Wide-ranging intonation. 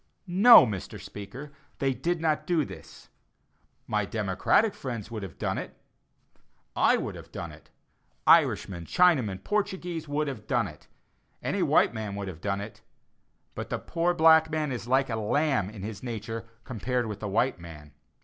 Yes: wide, 7.2 semitones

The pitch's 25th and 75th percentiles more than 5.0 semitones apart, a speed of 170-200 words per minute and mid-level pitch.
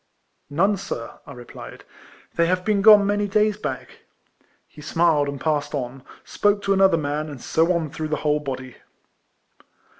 Yes: wide, 5.4 semitones; average, 175 wpm; medium, 160 Hz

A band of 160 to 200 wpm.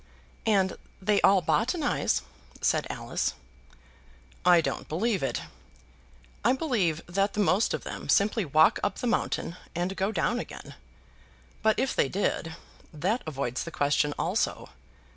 No: slow, 135 wpm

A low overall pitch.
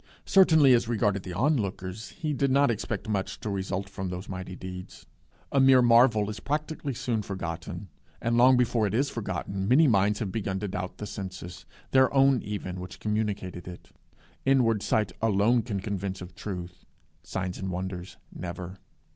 Yes: low, 100 Hz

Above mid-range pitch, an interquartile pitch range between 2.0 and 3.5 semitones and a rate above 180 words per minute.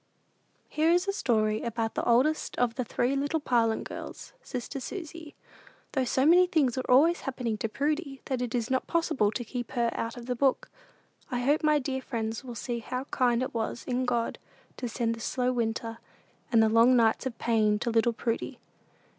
Yes: high, 245 Hz; average, 3.0 semitones; average, 200 wpm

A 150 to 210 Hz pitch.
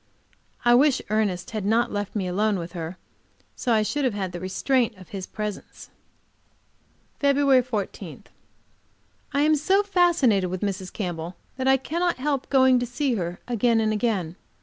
No: high, 220 Hz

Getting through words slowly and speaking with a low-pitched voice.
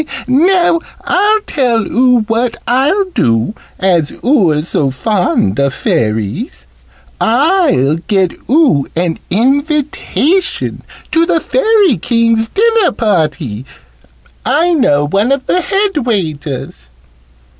No: slow, 105 wpm; high, 230 Hz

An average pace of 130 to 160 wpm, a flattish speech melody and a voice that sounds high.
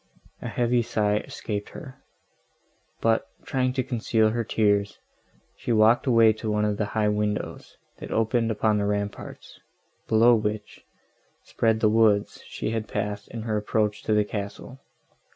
No: average, 150 wpm; narrow, 1.6 semitones; low, 110 Hz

